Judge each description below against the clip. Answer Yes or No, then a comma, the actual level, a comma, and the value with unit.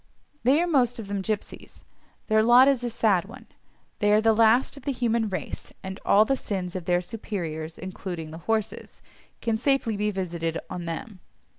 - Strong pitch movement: No, average, 4.4 semitones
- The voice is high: Yes, high, 215 Hz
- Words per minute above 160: Yes, average, 185 wpm